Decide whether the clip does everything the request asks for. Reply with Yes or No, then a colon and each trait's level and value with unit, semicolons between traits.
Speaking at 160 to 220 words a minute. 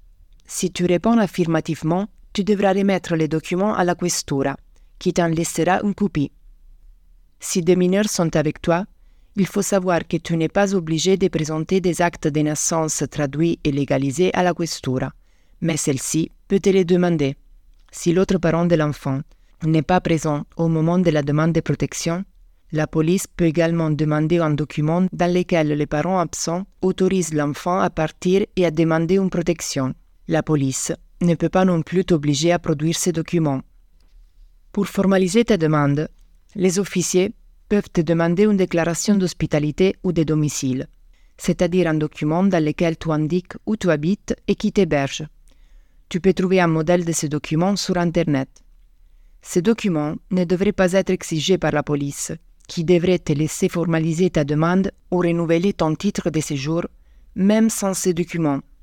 Yes: average, 165 wpm